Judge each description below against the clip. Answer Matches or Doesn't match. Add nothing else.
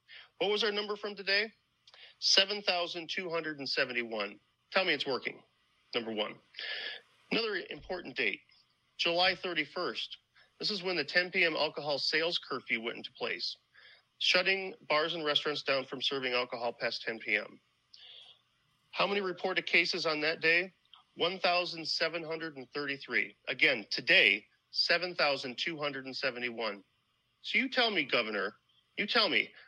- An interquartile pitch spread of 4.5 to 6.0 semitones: Matches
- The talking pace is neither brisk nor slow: Doesn't match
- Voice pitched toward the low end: Doesn't match